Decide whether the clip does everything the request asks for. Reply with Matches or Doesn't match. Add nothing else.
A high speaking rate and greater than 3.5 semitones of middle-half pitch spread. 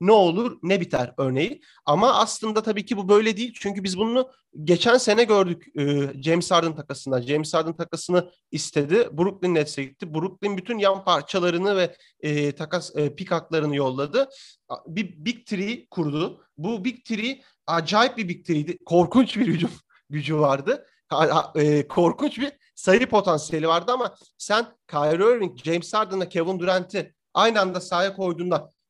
Matches